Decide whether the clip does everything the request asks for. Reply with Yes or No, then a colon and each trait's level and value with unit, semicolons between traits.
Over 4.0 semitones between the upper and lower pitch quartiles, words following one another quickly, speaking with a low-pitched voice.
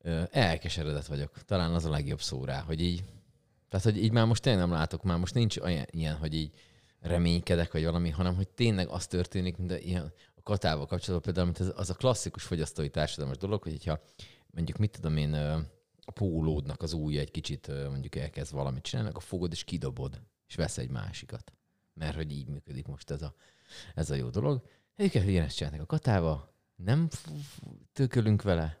Yes: average, 4.8 semitones; fast, 190 wpm; very low, 85 Hz